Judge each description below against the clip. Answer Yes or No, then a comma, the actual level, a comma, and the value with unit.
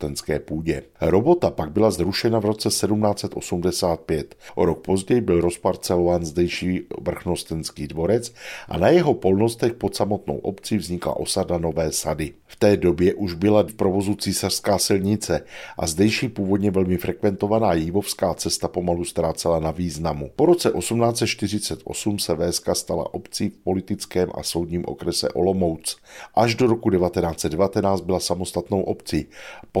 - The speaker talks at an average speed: Yes, average, 135 wpm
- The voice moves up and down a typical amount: Yes, average, 3.1 semitones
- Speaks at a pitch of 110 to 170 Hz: No, very low, 95 Hz